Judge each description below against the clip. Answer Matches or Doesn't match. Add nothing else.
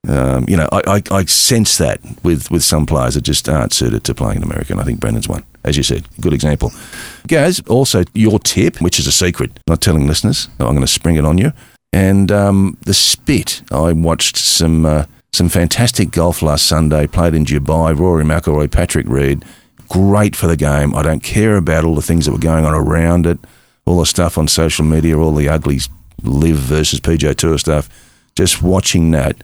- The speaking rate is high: Matches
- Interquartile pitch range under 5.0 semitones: Matches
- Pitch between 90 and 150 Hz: Doesn't match